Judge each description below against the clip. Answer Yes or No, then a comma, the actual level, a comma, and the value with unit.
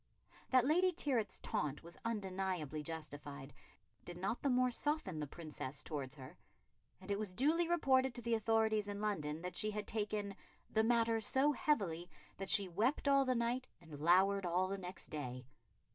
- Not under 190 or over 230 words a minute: No, average, 175 wpm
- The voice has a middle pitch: No, high, 200 Hz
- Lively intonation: Yes, wide, 6.3 semitones